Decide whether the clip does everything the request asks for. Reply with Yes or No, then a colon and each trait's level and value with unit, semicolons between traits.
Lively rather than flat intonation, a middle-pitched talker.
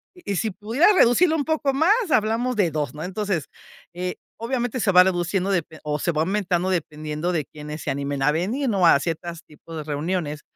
Yes: wide, 6.7 semitones; medium, 180 Hz